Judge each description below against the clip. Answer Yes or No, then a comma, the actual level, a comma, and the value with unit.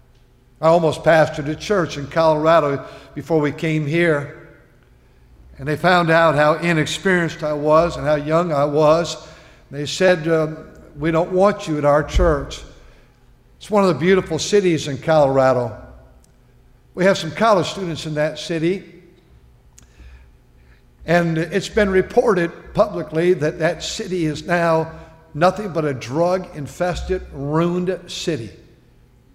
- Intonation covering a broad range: No, average, 3.1 semitones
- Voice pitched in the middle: Yes, medium, 160 Hz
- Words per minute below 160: Yes, average, 140 wpm